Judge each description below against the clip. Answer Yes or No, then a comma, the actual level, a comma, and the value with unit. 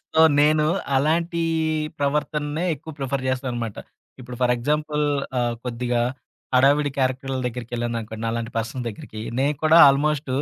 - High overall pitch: No, low, 130 Hz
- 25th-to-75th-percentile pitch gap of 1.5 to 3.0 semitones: No, average, 3.8 semitones